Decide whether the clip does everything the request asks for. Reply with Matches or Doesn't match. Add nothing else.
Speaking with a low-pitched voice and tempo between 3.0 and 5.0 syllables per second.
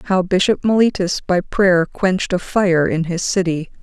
Doesn't match